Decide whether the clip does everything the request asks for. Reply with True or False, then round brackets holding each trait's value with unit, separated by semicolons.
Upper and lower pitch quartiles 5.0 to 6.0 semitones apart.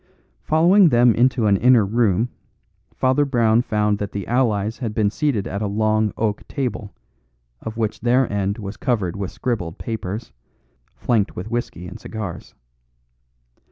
False (3.1 semitones)